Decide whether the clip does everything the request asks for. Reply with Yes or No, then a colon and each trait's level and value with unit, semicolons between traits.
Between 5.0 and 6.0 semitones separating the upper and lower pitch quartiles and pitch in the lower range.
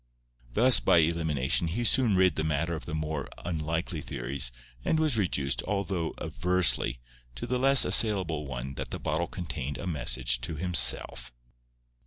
Yes: average, 5.3 semitones; very low, 80 Hz